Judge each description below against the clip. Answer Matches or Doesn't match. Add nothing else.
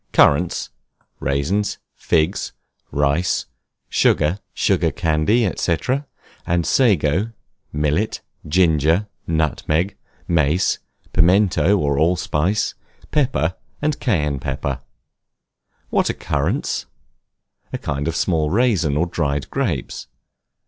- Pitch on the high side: Doesn't match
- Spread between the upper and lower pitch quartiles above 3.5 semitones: Matches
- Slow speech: Matches